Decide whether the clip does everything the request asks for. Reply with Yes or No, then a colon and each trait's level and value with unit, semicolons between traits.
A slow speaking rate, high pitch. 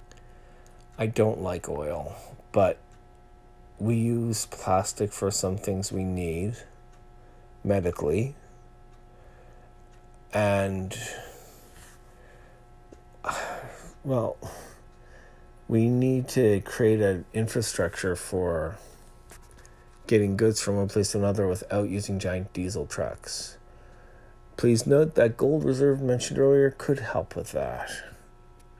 No: slow, 95 wpm; very low, 95 Hz